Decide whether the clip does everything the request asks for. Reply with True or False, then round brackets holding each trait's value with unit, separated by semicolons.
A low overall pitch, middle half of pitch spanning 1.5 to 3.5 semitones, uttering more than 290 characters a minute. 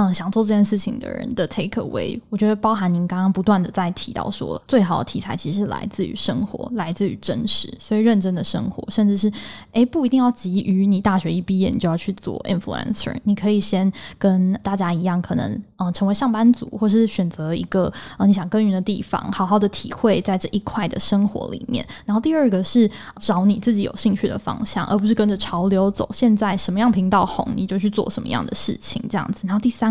False (205 Hz; 2.5 semitones; 370 characters per minute)